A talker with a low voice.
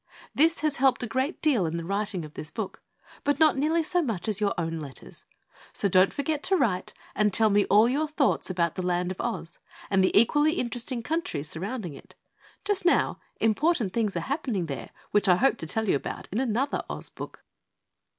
No: high, 220 Hz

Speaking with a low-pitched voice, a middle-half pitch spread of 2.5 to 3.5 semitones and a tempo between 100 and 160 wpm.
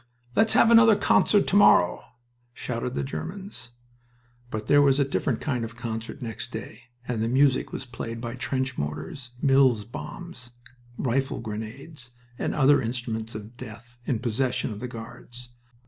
Yes: low, 125 Hz; average, 3.2 semitones; average, 155 wpm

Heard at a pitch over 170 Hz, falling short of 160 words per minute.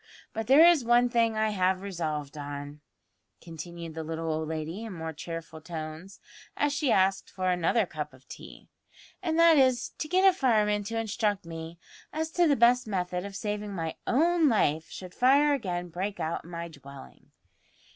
No: high, 190 Hz; average, 180 wpm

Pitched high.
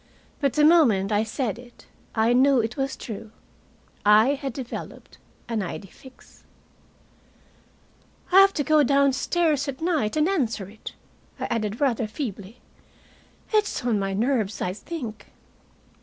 Yes: high, 245 Hz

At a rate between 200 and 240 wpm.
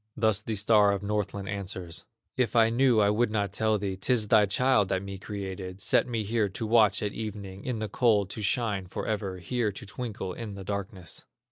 Yes: fast, 205 wpm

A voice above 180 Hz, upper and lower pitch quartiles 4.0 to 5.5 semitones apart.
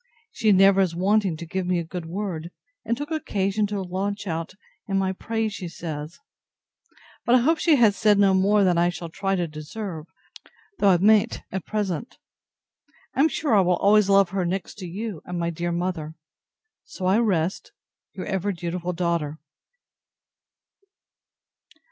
No: high, 190 Hz; average, 3.2 semitones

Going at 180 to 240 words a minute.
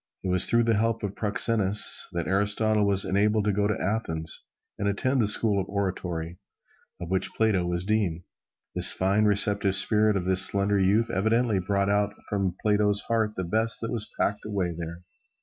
Yes: average, 185 wpm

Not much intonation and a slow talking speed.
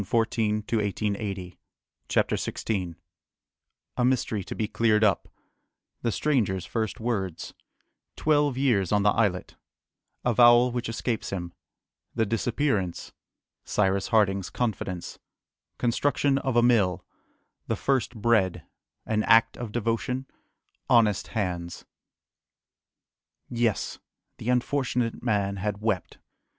No: average, 3.5 semitones; slow, 110 wpm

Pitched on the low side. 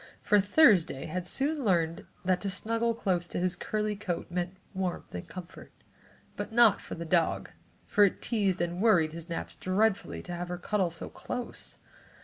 No: medium, 185 Hz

